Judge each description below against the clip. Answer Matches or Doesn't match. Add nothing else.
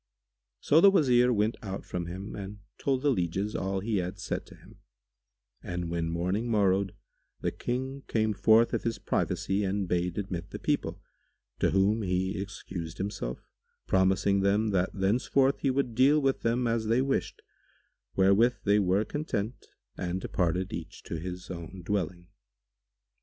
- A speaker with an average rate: Matches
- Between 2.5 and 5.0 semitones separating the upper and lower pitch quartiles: Matches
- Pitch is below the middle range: Matches